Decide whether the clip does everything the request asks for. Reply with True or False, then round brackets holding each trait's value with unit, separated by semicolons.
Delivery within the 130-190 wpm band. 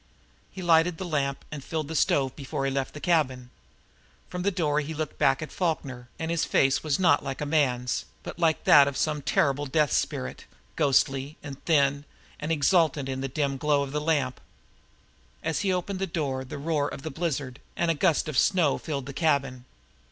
False (200 wpm)